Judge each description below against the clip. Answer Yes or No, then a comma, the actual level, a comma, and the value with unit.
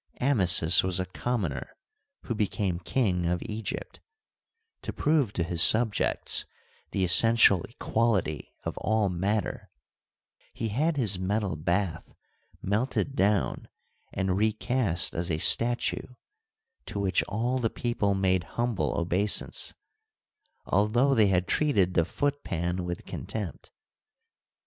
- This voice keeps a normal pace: No, slow, 120 wpm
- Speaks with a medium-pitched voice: No, low, 100 Hz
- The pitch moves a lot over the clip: No, average, 4.5 semitones